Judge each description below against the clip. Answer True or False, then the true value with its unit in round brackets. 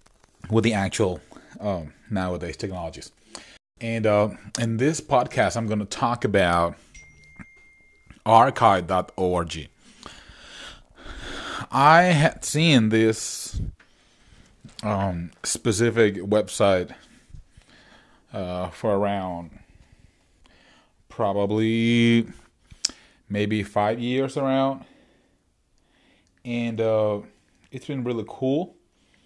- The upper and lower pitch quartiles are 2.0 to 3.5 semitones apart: False (4.3 semitones)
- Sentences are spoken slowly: True (80 wpm)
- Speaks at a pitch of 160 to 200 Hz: False (105 Hz)